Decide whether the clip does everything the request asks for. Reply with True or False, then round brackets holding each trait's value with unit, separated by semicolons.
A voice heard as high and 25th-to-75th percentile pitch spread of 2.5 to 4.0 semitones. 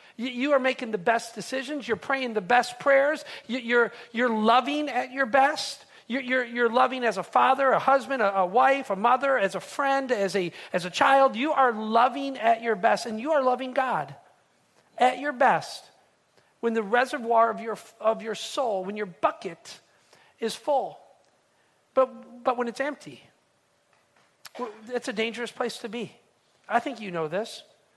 True (245 Hz; 3.1 semitones)